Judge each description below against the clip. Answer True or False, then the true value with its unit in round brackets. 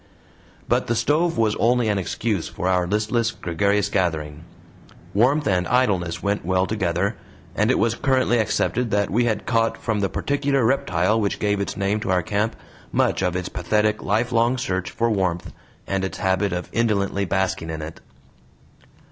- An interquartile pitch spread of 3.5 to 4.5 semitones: True (3.9 semitones)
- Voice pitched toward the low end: True (105 Hz)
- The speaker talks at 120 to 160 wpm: False (170 wpm)